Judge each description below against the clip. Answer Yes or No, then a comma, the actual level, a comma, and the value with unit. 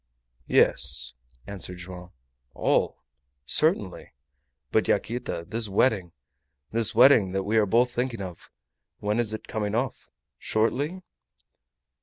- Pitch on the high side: No, low, 110 Hz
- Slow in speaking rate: Yes, slow, 115 wpm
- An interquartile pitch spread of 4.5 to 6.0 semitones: No, average, 3.8 semitones